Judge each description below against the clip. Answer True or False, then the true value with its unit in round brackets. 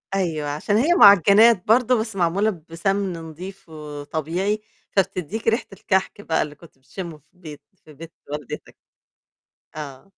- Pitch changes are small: False (4.7 semitones)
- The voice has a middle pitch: True (180 Hz)